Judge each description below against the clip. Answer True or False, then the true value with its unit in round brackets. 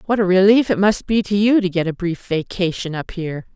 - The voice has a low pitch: False (190 Hz)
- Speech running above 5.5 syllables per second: True (5.7 syllables/s)